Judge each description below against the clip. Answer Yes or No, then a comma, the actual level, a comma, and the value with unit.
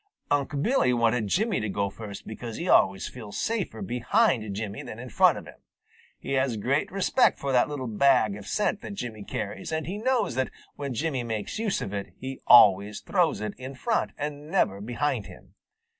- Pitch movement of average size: No, wide, 6.6 semitones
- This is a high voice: No, low, 125 Hz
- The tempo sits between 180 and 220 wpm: Yes, average, 195 wpm